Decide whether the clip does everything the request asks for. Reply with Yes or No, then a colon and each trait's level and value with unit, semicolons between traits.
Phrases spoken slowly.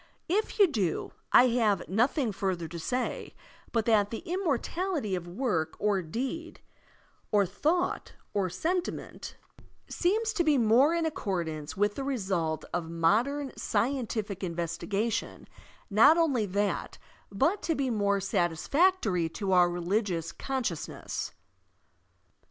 Yes: slow, 125 wpm